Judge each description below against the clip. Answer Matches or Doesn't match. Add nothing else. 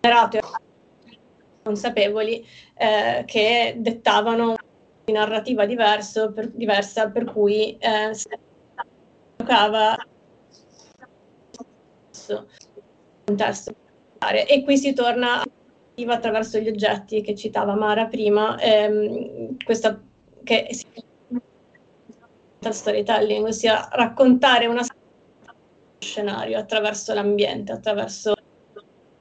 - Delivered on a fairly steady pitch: Matches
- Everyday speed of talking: Doesn't match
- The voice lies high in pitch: Matches